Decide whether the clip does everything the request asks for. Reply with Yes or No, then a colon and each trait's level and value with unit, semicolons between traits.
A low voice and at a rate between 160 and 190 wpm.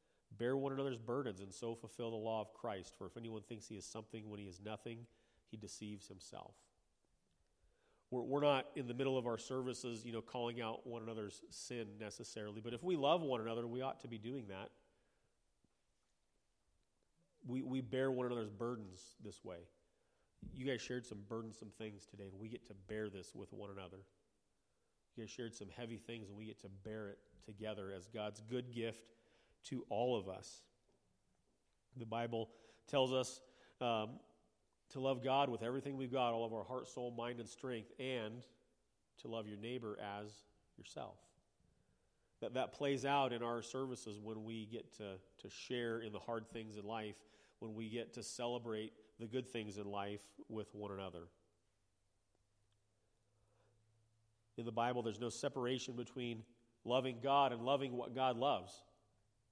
Yes: low, 115 Hz; average, 175 wpm